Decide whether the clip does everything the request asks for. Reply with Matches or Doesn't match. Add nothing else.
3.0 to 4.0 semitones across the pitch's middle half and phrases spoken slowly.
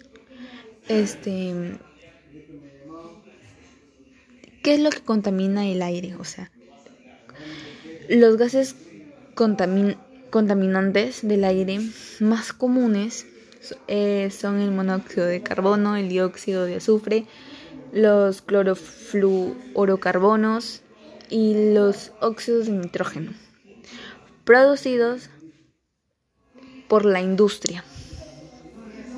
Matches